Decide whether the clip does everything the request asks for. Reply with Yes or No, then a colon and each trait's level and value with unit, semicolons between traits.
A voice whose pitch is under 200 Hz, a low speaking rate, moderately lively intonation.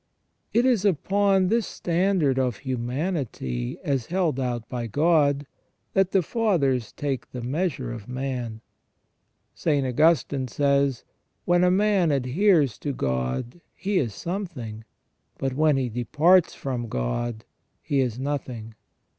No: medium, 140 Hz; slow, 130 wpm; wide, 6.4 semitones